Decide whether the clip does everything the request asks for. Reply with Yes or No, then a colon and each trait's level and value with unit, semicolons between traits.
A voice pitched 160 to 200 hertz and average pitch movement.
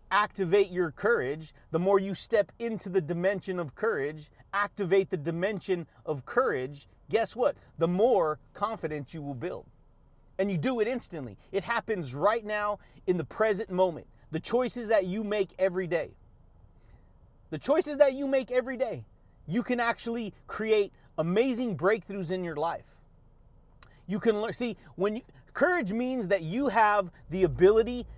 No: high, 190 Hz; wide, 6.0 semitones